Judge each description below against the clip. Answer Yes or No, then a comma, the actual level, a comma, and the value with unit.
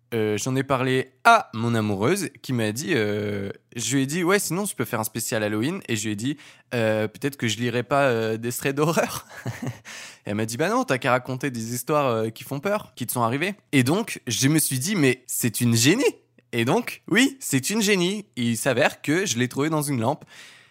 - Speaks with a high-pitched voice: No, low, 130 Hz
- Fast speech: Yes, fast, 240 wpm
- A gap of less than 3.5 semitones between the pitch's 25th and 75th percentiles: No, average, 4.3 semitones